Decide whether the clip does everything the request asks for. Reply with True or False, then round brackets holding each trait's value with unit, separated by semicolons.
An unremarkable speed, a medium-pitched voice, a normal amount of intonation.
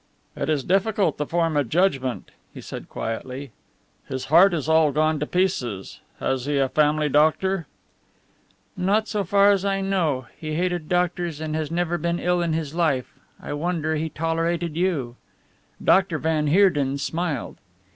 True (160 wpm; 160 Hz; 3.3 semitones)